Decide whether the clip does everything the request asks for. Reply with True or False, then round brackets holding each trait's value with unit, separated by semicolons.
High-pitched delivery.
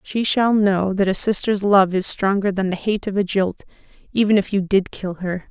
True (195 Hz)